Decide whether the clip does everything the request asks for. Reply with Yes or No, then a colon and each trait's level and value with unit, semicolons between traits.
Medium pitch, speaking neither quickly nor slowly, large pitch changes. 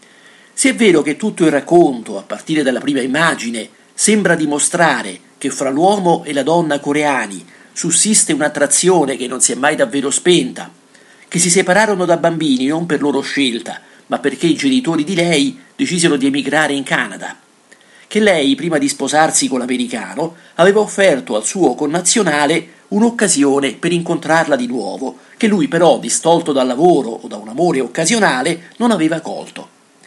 Yes: medium, 165 Hz; average, 160 wpm; wide, 5.7 semitones